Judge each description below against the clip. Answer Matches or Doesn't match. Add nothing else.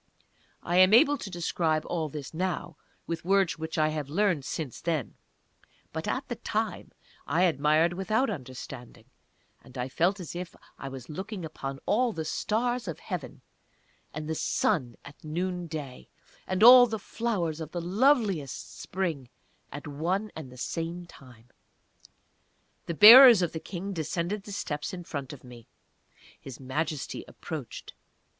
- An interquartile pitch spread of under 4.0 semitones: Doesn't match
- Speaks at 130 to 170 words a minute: Matches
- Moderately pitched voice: Matches